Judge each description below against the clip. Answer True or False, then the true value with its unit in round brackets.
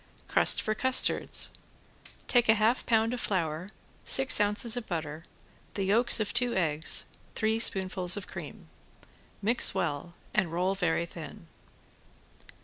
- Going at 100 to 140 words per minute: True (135 wpm)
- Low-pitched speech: False (195 Hz)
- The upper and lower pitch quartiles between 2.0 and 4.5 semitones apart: False (4.9 semitones)